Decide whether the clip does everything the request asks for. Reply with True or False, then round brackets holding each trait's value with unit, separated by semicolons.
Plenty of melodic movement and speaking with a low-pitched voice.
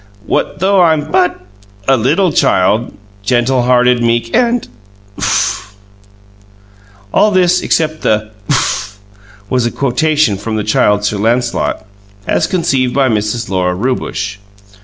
True (6.6 semitones; 120 Hz)